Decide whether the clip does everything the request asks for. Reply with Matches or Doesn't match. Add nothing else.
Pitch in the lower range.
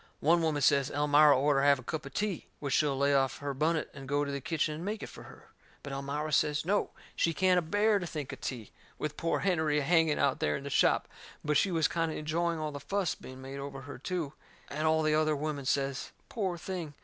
Doesn't match